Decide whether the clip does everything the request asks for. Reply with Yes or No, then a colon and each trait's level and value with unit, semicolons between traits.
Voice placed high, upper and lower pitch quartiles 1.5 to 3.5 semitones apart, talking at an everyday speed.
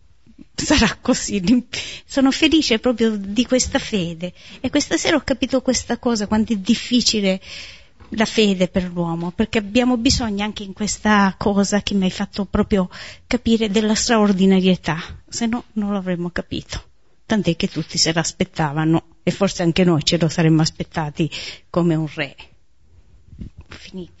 No: high, 200 Hz; average, 5.2 semitones; average, 145 wpm